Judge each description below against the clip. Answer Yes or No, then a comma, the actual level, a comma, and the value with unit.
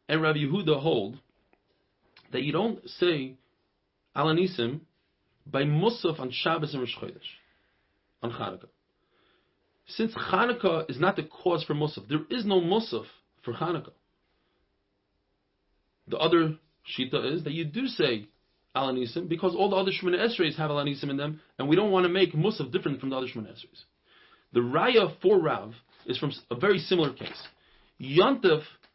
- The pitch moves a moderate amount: No, wide, 6.3 semitones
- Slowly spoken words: No, average, 155 wpm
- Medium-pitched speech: Yes, medium, 155 Hz